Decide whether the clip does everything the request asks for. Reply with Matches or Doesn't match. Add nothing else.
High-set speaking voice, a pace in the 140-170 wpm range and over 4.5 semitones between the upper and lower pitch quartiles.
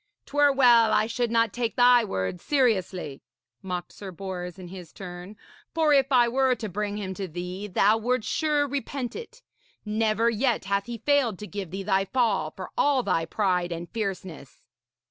Doesn't match